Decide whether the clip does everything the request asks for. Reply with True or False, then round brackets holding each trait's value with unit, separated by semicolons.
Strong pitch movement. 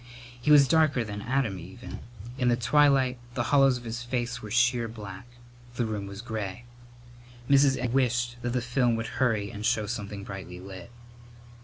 False (3.1 semitones)